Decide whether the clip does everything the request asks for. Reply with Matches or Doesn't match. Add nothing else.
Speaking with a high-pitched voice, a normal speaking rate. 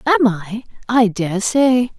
Matches